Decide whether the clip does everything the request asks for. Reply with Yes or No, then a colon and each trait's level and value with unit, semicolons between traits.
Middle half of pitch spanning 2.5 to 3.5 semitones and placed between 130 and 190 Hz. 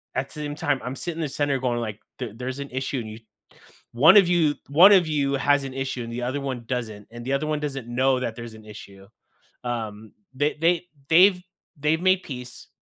No: average, 4.0 semitones; low, 135 Hz